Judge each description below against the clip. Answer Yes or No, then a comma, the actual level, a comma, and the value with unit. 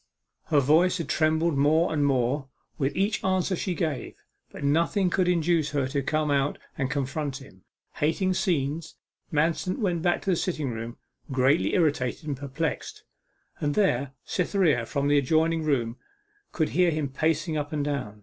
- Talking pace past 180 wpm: No, average, 165 wpm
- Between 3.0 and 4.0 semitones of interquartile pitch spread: Yes, average, 3.3 semitones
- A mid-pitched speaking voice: Yes, medium, 150 Hz